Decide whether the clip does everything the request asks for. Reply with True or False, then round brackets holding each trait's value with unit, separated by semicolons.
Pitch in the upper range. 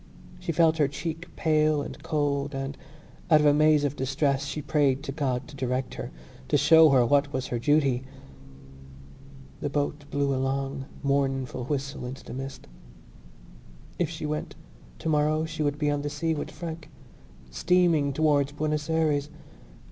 False (145 Hz)